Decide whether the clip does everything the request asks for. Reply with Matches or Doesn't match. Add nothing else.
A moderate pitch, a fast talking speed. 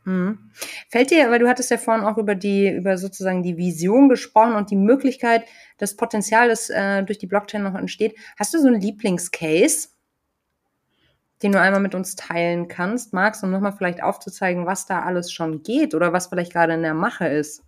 Doesn't match